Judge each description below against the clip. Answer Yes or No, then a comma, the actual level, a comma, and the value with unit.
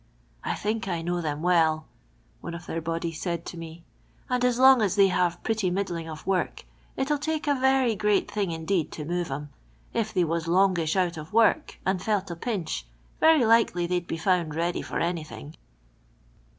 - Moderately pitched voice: Yes, medium, 180 Hz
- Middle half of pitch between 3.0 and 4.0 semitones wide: No, average, 4.4 semitones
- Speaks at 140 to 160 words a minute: No, average, 200 wpm